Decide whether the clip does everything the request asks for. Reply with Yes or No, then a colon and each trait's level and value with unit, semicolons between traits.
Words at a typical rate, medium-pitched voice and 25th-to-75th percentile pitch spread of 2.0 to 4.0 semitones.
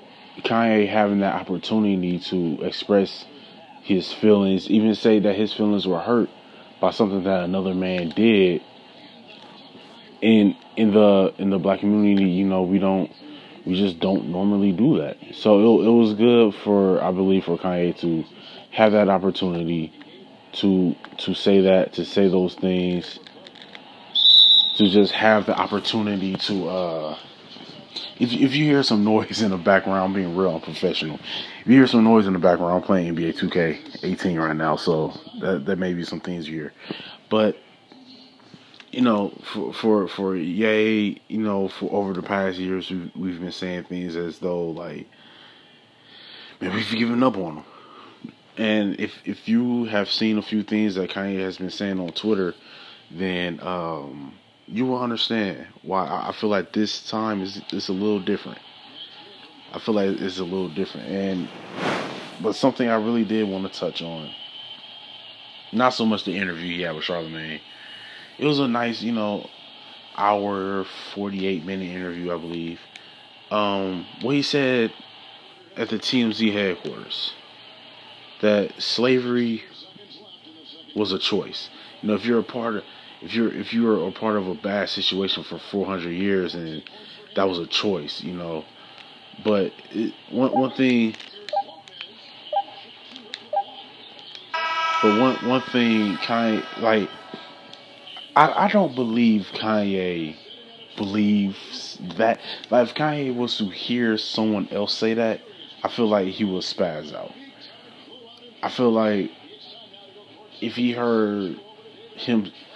No: average, 155 wpm; low, 100 Hz; average, 3.2 semitones